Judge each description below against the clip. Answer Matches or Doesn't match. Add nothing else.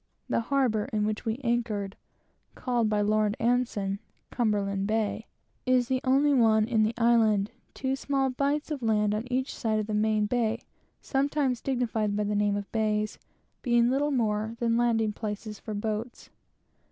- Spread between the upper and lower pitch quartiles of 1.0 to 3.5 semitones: Matches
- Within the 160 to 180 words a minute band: Matches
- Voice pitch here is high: Matches